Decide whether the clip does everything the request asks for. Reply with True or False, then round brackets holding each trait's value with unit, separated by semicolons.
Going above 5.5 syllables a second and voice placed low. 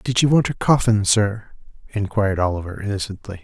True (5.7 syllables/s; 105 Hz)